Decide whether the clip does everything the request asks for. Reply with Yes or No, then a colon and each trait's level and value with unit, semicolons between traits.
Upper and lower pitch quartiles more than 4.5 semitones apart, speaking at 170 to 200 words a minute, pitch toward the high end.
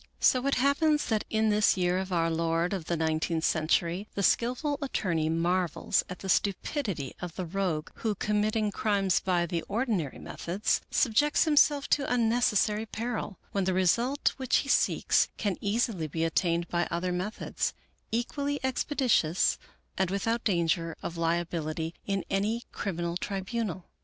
No: average, 5.1 semitones; average, 150 wpm; high, 195 Hz